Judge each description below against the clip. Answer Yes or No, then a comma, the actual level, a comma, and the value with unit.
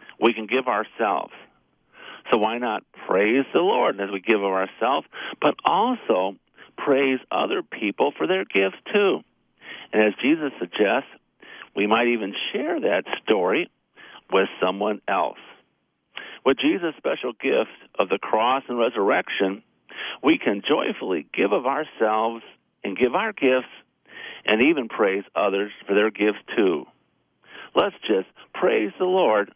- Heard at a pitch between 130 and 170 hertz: No, low, 110 Hz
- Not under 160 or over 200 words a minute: No, average, 140 wpm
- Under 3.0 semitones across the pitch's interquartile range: No, average, 4.2 semitones